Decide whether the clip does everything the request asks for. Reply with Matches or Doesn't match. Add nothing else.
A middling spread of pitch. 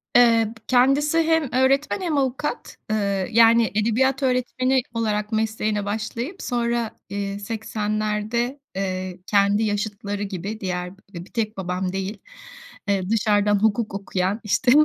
Matches